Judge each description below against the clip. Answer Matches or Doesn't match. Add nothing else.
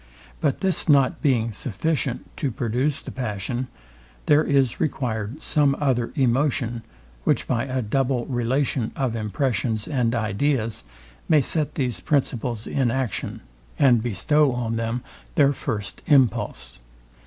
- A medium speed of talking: Doesn't match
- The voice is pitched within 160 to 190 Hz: Doesn't match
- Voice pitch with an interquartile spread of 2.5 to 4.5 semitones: Matches